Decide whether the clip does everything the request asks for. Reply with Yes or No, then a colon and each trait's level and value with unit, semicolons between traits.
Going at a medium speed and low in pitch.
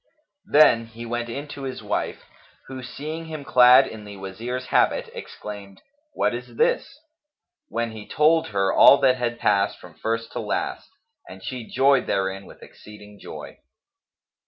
Yes: average, 160 wpm; low, 120 Hz